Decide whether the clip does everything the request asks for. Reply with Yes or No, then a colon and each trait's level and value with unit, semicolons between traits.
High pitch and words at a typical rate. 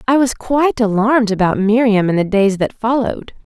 Yes: high, 225 Hz; average, 185 wpm